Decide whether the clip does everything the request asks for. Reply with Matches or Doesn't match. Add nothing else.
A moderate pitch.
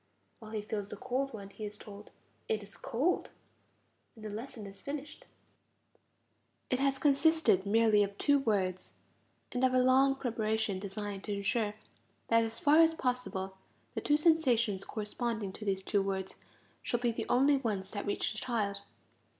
Doesn't match